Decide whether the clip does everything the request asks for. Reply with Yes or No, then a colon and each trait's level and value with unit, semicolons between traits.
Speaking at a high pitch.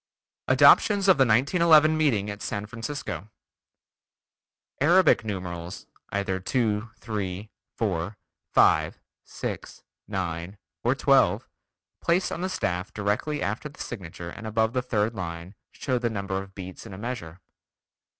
No: low, 105 Hz